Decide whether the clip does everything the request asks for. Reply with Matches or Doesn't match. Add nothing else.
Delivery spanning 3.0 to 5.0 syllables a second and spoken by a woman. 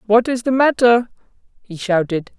Matches